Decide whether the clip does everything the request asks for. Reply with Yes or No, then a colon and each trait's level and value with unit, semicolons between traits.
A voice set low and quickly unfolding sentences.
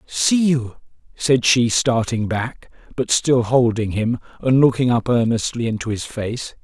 No: low, 120 Hz; average, 155 wpm